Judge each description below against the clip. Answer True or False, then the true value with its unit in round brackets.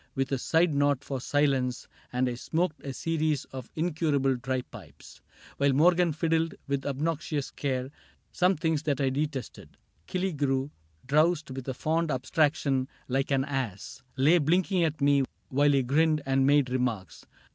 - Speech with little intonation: False (3.2 semitones)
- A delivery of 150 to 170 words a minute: True (155 wpm)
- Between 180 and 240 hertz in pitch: False (140 Hz)